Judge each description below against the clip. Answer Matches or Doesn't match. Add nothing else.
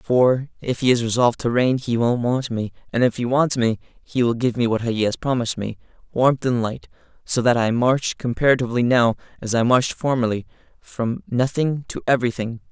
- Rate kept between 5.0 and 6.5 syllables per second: Matches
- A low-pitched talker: Matches